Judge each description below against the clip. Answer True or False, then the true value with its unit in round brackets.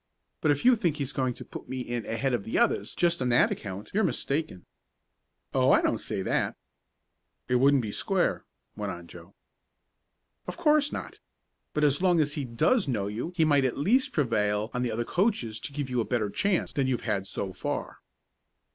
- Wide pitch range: True (6.2 semitones)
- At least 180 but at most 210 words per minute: True (200 wpm)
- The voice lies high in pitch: False (135 Hz)